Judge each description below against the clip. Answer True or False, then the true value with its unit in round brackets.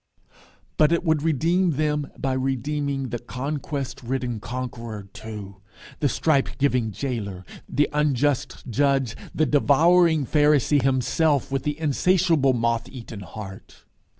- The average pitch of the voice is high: False (135 Hz)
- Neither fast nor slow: False (125 wpm)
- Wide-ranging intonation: False (3.8 semitones)